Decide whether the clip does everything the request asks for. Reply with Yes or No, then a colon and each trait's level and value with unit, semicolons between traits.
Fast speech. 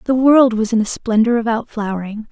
Yes: fast, 235 wpm